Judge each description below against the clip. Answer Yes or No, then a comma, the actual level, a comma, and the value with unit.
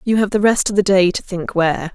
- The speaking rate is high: Yes, fast, 310 wpm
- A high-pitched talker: Yes, high, 195 Hz